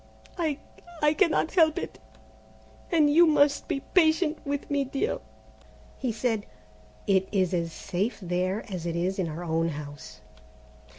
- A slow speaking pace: No, average, 150 wpm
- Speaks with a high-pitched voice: Yes, high, 225 Hz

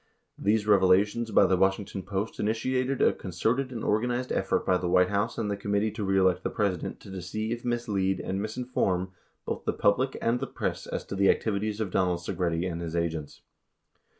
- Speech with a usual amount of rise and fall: Yes, average, 3.3 semitones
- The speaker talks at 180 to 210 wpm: Yes, average, 190 wpm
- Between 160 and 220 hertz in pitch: No, low, 100 Hz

